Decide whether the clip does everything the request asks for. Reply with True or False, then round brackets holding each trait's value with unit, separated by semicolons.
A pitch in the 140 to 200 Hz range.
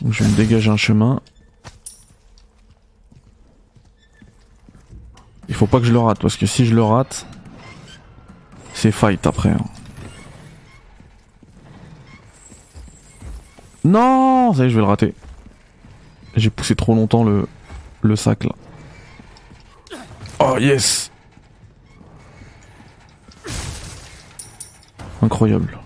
False (110 Hz)